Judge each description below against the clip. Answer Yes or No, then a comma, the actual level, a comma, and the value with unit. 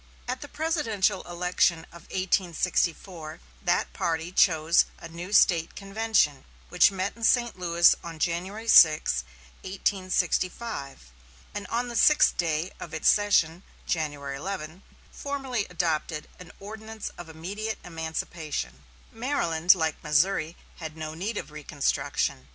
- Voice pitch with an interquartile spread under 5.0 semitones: Yes, average, 4.2 semitones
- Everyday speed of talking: No, slow, 125 wpm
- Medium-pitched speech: Yes, medium, 175 Hz